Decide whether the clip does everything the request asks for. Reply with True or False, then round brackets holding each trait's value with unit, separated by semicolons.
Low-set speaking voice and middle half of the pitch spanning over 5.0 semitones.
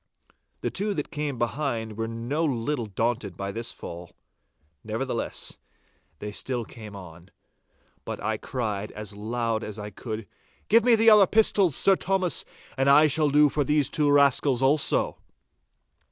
True (125 Hz; 5.6 semitones)